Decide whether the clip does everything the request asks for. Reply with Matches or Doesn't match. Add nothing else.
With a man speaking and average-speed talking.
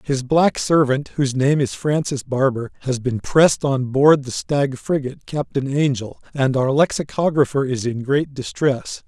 Matches